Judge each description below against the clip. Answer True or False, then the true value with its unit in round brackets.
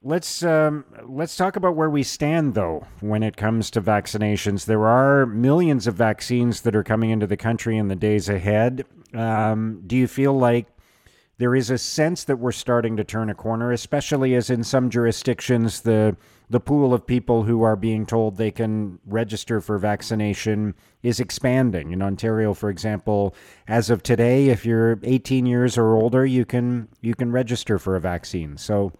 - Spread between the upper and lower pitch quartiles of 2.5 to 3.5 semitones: True (2.9 semitones)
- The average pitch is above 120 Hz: False (115 Hz)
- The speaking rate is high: False (180 wpm)